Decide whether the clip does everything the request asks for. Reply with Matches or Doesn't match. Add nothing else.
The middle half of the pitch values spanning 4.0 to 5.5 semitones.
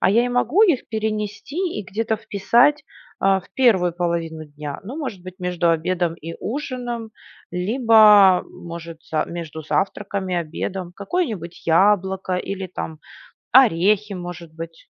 Matches